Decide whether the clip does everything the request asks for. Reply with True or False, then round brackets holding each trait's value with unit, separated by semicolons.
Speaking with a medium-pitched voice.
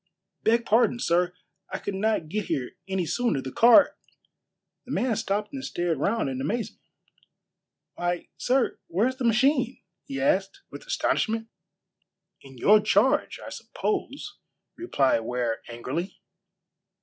False (210 Hz)